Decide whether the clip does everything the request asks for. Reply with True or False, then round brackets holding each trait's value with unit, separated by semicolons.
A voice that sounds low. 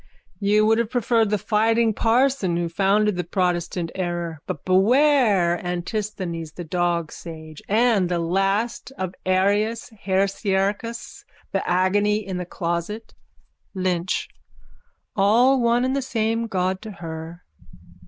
False (195 Hz)